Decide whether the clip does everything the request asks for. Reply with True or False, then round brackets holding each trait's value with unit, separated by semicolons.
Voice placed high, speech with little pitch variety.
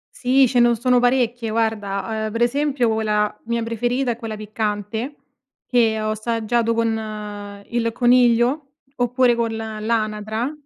True (230 Hz; 2.0 semitones)